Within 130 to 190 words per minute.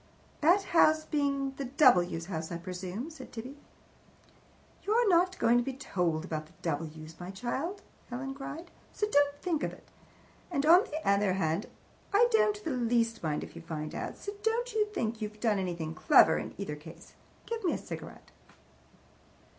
Yes: average, 175 wpm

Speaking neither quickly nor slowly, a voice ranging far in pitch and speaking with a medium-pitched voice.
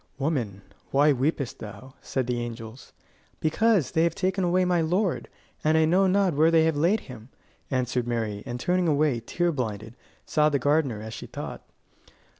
Yes: average, 175 wpm; wide, 5.8 semitones; medium, 145 Hz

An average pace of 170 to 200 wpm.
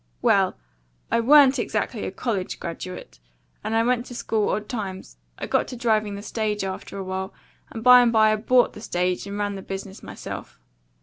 Yes: average, 190 wpm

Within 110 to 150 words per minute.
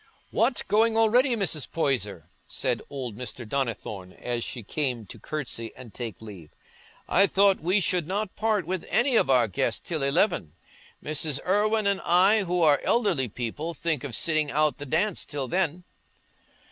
No: average, 165 wpm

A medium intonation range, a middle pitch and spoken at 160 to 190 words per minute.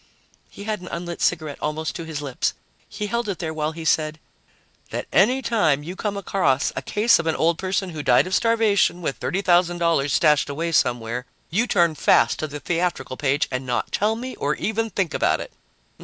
No: average, 4.9 semitones; medium, 170 Hz; average, 200 wpm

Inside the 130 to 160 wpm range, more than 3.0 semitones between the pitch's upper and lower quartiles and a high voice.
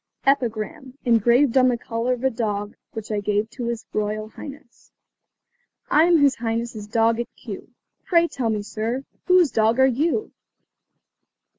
Yes: average, 155 wpm; average, 3.4 semitones; high, 235 Hz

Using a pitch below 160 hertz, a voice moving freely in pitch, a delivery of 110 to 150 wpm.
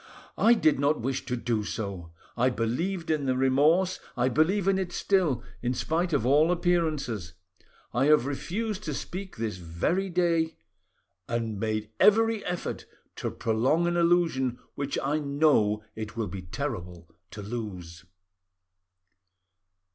Yes: medium, 140 Hz; wide, 7.5 semitones; average, 140 wpm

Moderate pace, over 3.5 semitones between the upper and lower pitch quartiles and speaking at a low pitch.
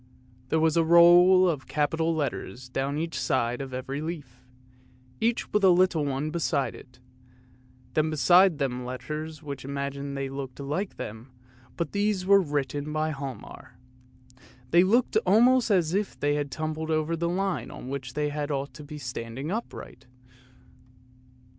No: average, 160 wpm; average, 3.9 semitones; medium, 150 Hz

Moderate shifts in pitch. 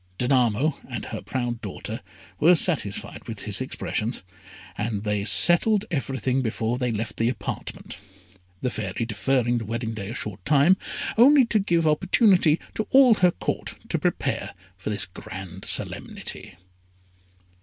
No: wide, 7.2 semitones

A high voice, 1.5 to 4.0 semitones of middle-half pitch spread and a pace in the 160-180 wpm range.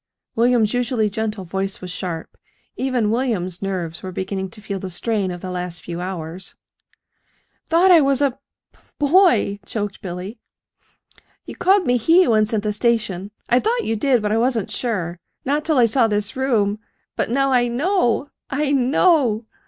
No: high, 220 Hz; wide, 5.5 semitones; average, 170 wpm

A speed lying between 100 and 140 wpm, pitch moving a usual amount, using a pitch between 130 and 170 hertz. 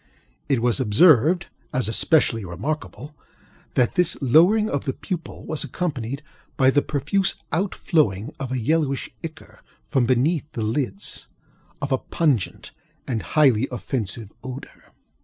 Yes: slow, 135 wpm; average, 4.8 semitones; low, 135 Hz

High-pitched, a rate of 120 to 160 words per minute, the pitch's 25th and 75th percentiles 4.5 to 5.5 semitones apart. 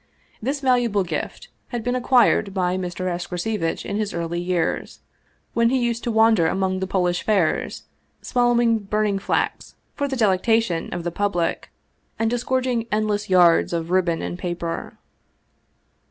Yes: high, 200 Hz; average, 150 wpm; average, 4.8 semitones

